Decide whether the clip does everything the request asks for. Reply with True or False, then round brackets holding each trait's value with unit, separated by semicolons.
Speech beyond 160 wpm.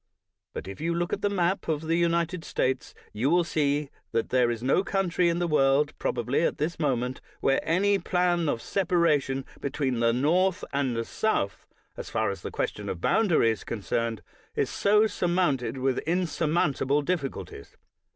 True (180 wpm)